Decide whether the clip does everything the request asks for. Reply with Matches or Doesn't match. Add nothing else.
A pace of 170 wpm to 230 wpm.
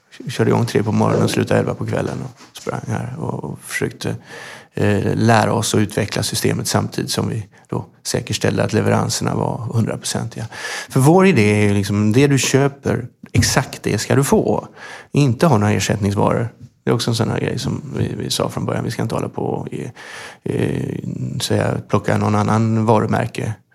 Matches